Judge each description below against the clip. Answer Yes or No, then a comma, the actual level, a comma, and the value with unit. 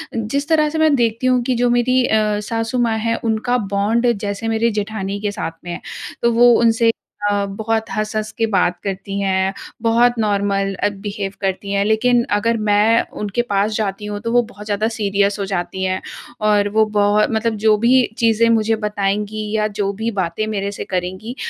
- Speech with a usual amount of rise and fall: No, narrow, 2.3 semitones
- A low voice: No, high, 215 Hz